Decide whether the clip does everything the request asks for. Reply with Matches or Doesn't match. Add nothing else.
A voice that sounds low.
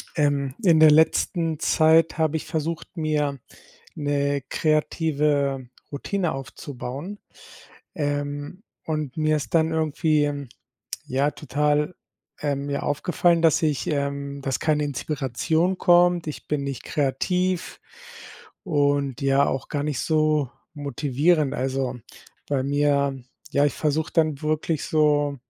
Doesn't match